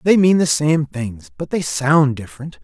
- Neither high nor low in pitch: Yes, medium, 145 Hz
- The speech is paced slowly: No, fast, 205 wpm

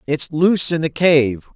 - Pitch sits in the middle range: Yes, medium, 155 Hz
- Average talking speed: Yes, average, 195 wpm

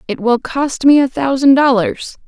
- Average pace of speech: Yes, average, 185 wpm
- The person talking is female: Yes, female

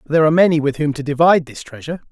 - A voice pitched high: No, medium, 150 Hz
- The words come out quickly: Yes, fast, 285 wpm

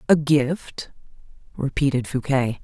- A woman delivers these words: Yes, female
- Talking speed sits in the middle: No, slow, 90 wpm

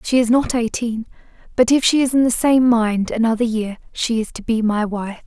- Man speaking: No, female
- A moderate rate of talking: No, fast, 230 wpm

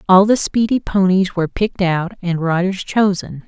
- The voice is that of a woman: Yes, female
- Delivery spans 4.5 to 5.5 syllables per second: Yes, 5.0 syllables/s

